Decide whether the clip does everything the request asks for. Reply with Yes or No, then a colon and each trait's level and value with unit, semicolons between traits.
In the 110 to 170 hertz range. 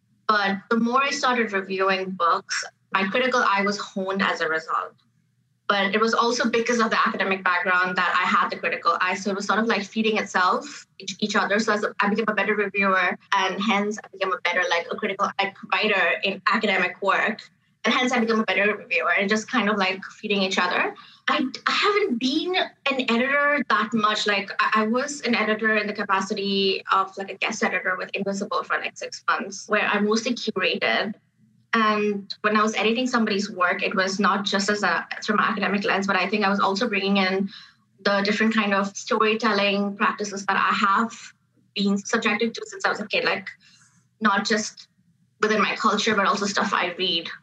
No: high, 205 Hz